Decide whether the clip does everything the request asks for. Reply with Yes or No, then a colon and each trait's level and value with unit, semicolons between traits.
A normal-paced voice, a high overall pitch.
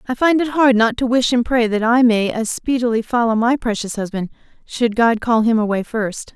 No: fast, 225 wpm; high, 235 Hz